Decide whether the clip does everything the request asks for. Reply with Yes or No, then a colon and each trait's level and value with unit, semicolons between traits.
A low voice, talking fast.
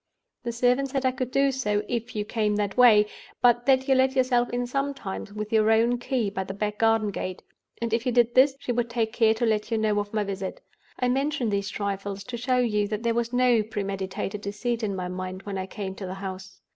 No: high, 225 Hz; fast, 240 wpm